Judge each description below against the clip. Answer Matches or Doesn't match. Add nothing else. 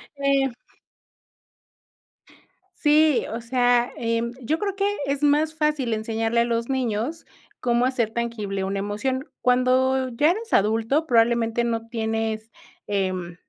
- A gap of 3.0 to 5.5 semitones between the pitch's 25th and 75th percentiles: Matches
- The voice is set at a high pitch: Matches